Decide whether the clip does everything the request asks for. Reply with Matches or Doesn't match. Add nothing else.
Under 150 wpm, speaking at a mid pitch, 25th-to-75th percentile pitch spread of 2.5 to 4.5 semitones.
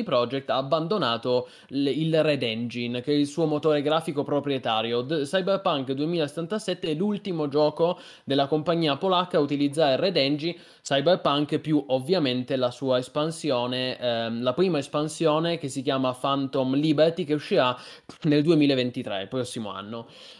Matches